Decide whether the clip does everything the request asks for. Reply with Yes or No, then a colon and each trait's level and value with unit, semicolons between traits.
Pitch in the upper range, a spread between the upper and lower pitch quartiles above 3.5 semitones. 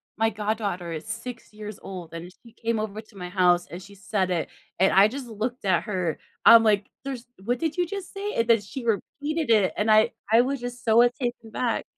Yes: high, 220 Hz; average, 3.9 semitones